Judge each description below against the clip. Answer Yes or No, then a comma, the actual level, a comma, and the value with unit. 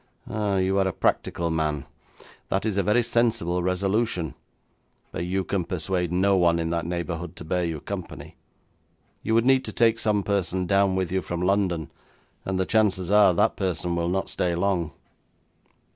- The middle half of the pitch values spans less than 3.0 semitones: Yes, narrow, 2.6 semitones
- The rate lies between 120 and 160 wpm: No, average, 175 wpm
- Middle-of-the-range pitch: No, very low, 95 Hz